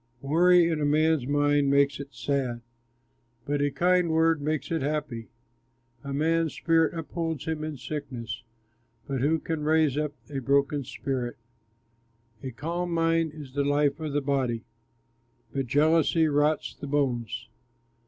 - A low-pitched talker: No, medium, 145 Hz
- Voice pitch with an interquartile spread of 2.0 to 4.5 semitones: Yes, narrow, 2.6 semitones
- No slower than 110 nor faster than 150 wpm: Yes, average, 145 wpm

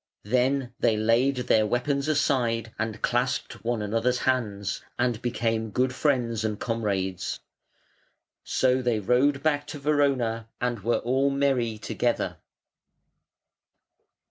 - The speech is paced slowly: Yes, slow, 115 wpm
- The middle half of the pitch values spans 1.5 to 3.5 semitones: Yes, average, 2.9 semitones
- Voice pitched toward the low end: Yes, low, 120 Hz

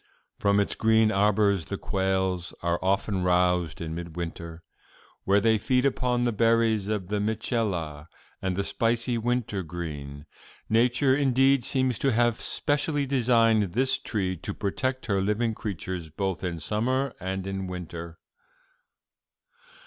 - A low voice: Yes, low, 100 Hz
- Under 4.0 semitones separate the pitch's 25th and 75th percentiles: No, average, 4.8 semitones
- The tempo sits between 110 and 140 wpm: Yes, slow, 135 wpm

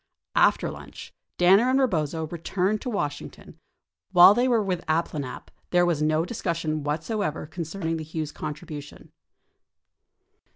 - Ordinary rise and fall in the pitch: Yes, average, 4.0 semitones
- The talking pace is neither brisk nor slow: No, slow, 130 wpm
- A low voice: No, medium, 165 Hz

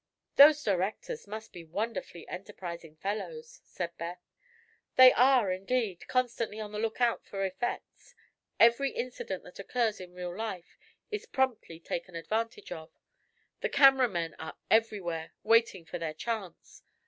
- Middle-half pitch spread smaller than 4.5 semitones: No, average, 5.2 semitones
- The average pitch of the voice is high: Yes, high, 210 Hz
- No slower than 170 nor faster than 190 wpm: No, slow, 135 wpm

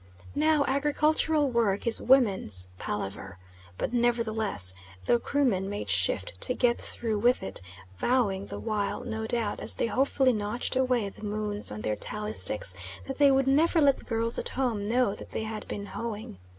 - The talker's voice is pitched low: No, high, 230 Hz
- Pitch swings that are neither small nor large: Yes, average, 4.2 semitones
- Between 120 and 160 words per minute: No, average, 175 wpm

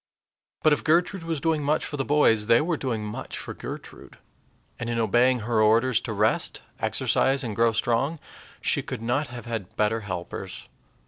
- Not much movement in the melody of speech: No, average, 4.6 semitones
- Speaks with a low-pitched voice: Yes, low, 120 Hz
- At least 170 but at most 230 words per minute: Yes, average, 180 wpm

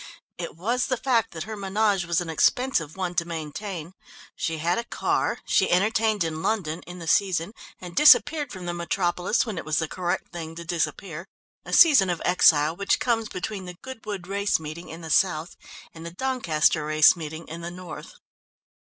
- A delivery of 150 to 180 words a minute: No, average, 190 wpm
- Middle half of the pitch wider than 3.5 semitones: Yes, average, 4.1 semitones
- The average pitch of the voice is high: No, medium, 175 Hz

